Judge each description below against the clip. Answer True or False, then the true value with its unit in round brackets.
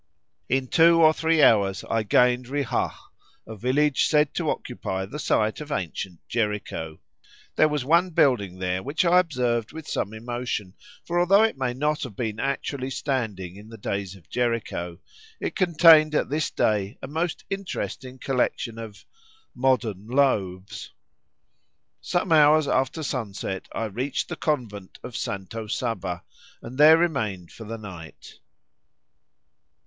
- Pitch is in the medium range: False (125 Hz)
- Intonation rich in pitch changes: True (6.4 semitones)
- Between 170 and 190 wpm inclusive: False (145 wpm)